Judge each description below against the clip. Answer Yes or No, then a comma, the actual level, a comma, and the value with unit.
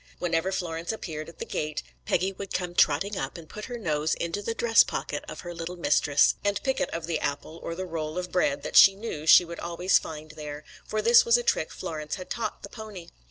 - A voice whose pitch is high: No, medium, 170 Hz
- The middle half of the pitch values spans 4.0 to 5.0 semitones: Yes, average, 4.3 semitones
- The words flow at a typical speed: No, fast, 235 wpm